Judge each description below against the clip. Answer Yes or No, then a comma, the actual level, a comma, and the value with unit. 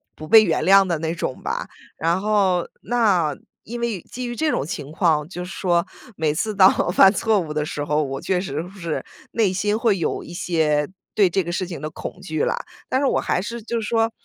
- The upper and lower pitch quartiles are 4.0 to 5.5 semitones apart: Yes, average, 5.1 semitones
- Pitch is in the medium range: Yes, medium, 180 Hz